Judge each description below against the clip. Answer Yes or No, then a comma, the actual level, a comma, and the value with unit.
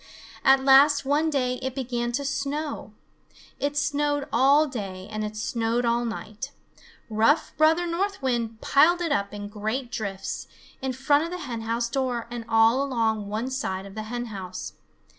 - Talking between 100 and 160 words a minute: No, average, 170 wpm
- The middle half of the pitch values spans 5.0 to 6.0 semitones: No, average, 4.3 semitones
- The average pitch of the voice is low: No, high, 245 Hz